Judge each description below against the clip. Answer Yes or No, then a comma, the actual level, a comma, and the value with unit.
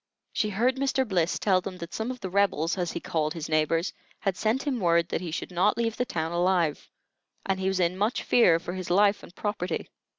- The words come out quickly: Yes, fast, 230 wpm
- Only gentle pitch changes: No, average, 3.8 semitones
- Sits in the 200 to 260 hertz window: No, medium, 185 Hz